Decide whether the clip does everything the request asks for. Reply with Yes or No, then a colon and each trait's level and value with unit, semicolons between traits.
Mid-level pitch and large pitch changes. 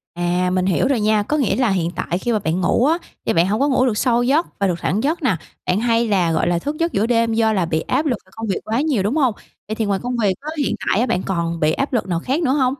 No: high, 220 Hz; wide, 5.7 semitones